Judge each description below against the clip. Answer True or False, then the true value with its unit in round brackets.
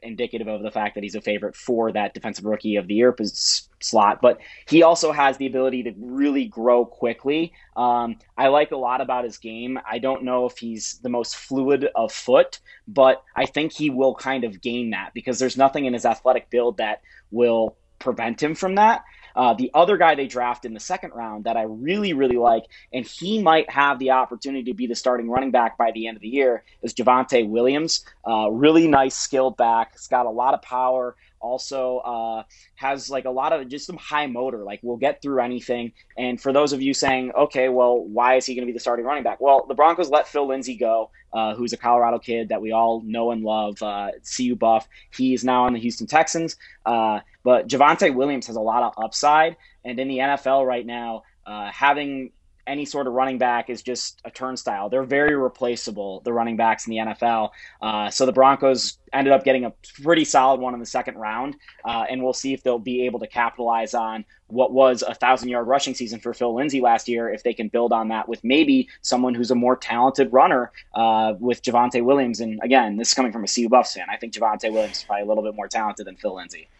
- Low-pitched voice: True (125 Hz)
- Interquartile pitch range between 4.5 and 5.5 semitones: False (2.7 semitones)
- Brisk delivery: True (225 wpm)